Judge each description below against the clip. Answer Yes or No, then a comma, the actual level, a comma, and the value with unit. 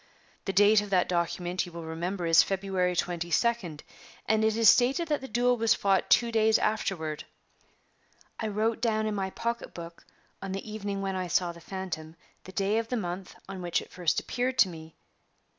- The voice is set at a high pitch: Yes, high, 195 Hz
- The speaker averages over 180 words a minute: Yes, average, 190 wpm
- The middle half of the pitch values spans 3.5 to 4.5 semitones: Yes, average, 3.8 semitones